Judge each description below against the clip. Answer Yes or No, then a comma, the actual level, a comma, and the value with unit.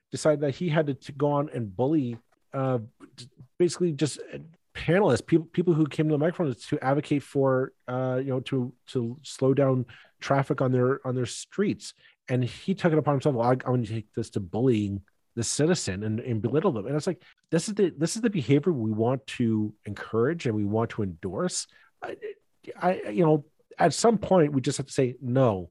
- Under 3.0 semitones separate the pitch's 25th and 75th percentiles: No, average, 4.6 semitones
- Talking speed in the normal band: No, fast, 210 wpm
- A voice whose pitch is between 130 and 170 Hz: Yes, low, 135 Hz